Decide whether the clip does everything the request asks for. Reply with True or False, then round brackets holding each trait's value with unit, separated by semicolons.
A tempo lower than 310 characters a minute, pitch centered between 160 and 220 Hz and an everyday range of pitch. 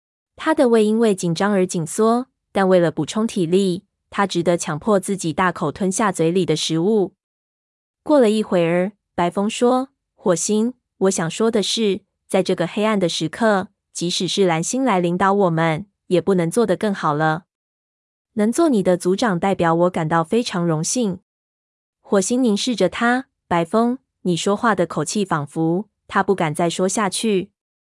True (240 characters per minute; 190 Hz; 4.0 semitones)